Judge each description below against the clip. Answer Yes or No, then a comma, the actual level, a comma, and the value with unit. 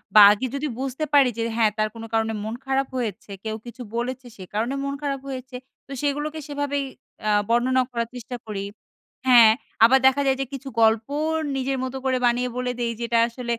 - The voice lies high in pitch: Yes, very high, 250 Hz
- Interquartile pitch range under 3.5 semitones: Yes, average, 2.8 semitones